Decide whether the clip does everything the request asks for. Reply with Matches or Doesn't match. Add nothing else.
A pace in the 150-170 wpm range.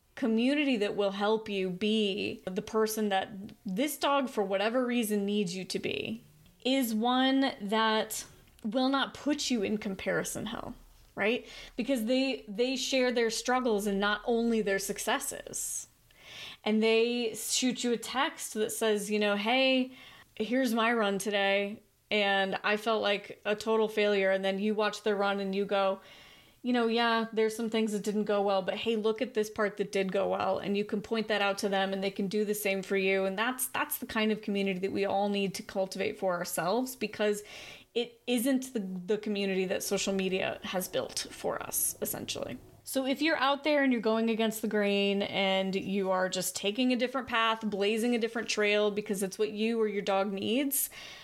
Doesn't match